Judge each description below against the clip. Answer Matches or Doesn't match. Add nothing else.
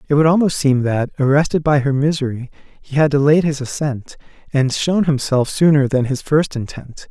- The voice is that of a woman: Doesn't match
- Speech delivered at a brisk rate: Doesn't match